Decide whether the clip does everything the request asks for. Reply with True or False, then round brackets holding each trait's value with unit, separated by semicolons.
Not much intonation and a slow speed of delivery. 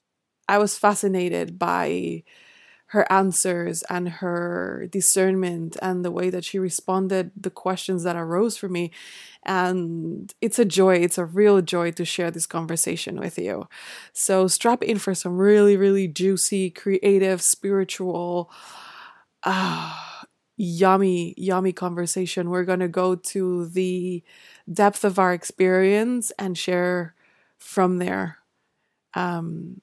True (1.6 semitones; 130 wpm)